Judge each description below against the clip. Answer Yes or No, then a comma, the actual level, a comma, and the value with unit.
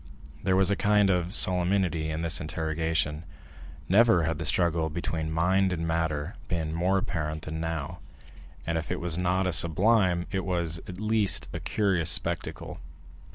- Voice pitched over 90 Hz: No, very low, 85 Hz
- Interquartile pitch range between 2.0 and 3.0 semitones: Yes, average, 2.7 semitones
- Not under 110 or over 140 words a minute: No, average, 160 wpm